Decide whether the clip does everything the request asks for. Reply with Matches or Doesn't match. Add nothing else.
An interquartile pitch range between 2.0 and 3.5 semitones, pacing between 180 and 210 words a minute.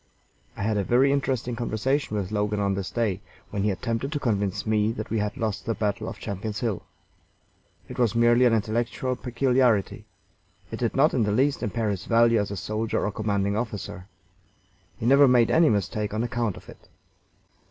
Matches